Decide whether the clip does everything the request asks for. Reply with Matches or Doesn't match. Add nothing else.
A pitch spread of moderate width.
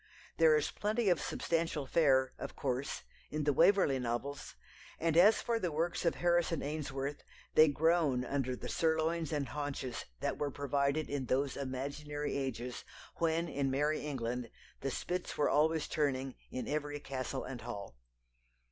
Matches